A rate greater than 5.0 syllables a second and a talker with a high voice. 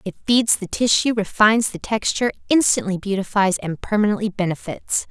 Yes: 5.5 syllables/s; high, 205 Hz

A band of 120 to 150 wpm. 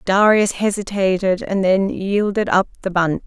Yes: average, 145 wpm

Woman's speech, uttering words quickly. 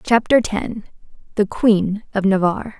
No: female; slow, 130 wpm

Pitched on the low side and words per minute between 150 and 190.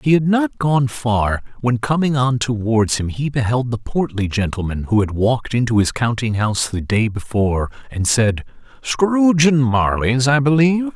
Yes: low, 125 Hz; average, 175 wpm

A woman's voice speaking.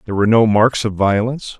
No: male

